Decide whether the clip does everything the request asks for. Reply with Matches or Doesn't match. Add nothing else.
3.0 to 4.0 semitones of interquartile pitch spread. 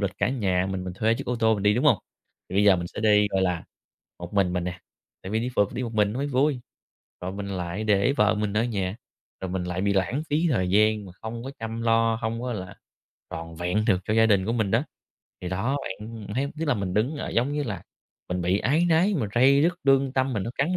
Doesn't match